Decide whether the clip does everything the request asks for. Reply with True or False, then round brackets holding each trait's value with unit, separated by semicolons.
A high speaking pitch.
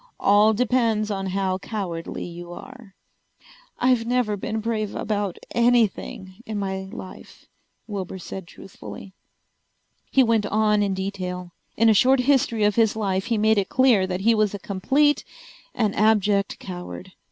True (210 Hz)